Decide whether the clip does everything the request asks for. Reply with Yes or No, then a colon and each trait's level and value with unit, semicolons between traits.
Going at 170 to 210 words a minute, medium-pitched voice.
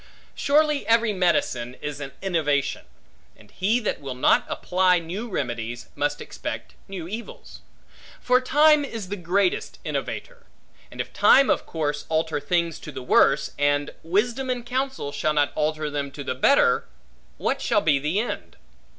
No: average, 160 wpm; medium, 175 Hz